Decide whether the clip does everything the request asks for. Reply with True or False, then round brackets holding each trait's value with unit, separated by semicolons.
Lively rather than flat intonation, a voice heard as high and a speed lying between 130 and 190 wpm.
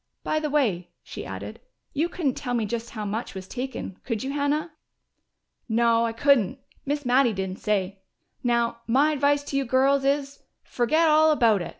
False (4.0 semitones; 255 Hz; 180 wpm)